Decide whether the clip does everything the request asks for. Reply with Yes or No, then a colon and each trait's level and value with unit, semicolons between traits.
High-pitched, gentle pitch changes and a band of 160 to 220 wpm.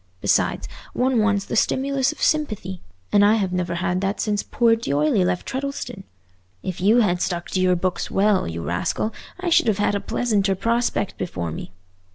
No: high, 200 Hz; average, 4.3 semitones; average, 185 wpm